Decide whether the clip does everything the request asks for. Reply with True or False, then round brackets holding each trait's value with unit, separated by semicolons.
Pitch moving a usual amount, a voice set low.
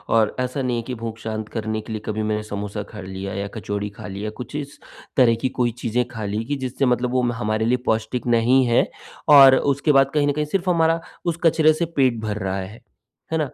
True (4.2 semitones; 115 Hz)